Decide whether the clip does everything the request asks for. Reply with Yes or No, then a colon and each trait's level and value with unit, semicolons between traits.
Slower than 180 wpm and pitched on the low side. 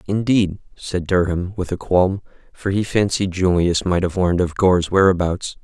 Yes: average, 170 wpm; very low, 90 Hz